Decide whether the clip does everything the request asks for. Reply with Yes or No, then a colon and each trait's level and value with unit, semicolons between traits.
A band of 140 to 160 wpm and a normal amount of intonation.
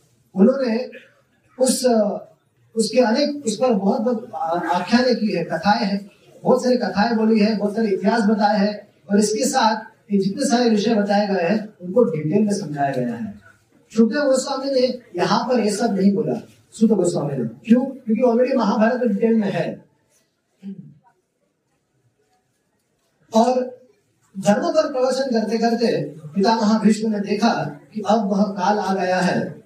Yes: average, 150 wpm; average, 3.3 semitones